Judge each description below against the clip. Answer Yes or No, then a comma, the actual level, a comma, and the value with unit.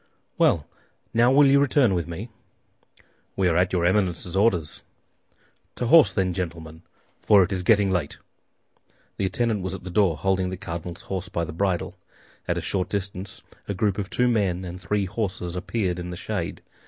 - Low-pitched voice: Yes, very low, 95 Hz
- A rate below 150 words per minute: No, average, 180 wpm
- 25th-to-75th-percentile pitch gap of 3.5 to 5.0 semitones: No, average, 2.7 semitones